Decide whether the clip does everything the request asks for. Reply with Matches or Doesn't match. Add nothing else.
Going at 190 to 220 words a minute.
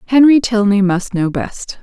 Doesn't match